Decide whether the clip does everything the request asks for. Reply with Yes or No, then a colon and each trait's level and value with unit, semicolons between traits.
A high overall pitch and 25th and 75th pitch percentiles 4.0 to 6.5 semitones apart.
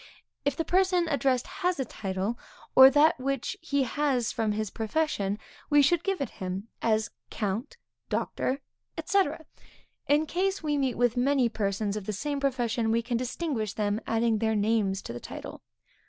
Yes: high, 245 Hz; average, 5.2 semitones